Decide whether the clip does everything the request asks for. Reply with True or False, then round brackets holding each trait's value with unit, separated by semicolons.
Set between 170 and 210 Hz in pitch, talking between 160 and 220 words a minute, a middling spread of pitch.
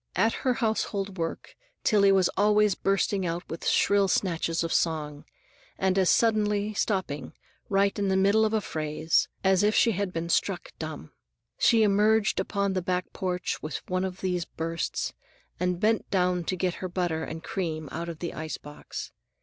True (185 Hz; 175 wpm; 3.4 semitones)